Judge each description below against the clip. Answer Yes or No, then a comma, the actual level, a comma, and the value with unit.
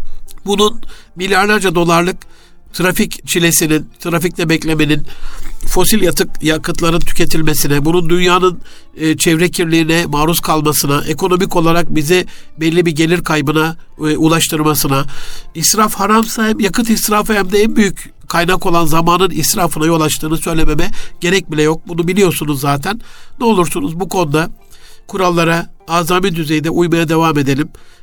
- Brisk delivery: No, average, 120 wpm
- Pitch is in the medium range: Yes, medium, 170 Hz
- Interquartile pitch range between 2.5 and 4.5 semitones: Yes, average, 2.8 semitones